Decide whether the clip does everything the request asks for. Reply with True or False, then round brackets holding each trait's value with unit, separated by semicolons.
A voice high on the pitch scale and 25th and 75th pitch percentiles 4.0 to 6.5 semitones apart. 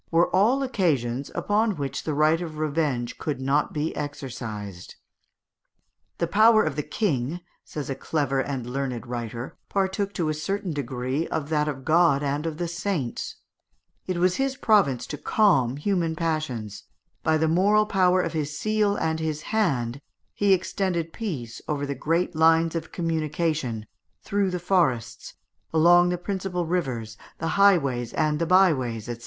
False (160 Hz; 5.0 semitones)